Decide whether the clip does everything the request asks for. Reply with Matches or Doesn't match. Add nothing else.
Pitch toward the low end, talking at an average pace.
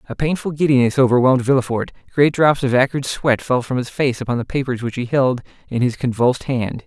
Doesn't match